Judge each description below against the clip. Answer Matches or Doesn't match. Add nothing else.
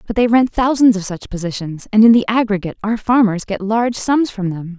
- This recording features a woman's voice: Matches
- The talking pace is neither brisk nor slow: Doesn't match